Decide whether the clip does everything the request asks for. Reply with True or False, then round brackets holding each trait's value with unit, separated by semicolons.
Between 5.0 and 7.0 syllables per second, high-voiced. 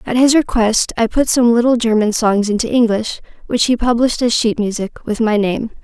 True (5.4 syllables/s; 230 Hz)